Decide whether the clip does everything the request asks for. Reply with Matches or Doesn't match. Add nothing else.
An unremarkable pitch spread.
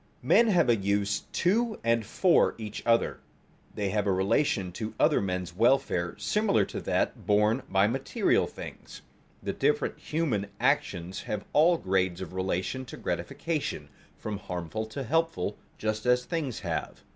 Doesn't match